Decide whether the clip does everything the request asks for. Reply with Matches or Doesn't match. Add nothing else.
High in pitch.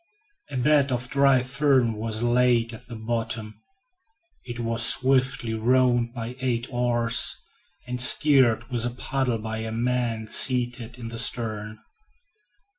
Doesn't match